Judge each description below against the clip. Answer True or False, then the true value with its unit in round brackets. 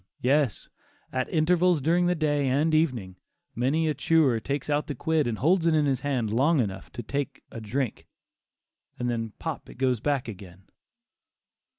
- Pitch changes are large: False (4.6 semitones)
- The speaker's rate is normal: True (175 wpm)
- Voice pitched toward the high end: False (140 Hz)